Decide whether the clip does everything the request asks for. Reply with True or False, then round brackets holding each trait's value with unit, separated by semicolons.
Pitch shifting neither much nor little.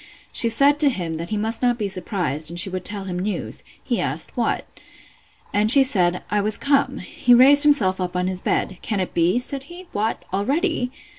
False (6.2 semitones)